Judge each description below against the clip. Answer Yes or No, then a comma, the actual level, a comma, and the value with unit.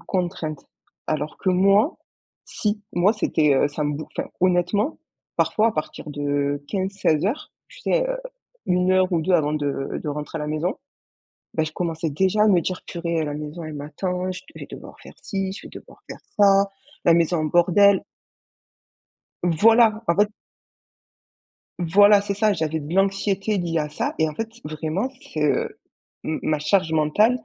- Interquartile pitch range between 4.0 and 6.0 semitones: Yes, average, 4.4 semitones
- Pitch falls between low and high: Yes, medium, 175 Hz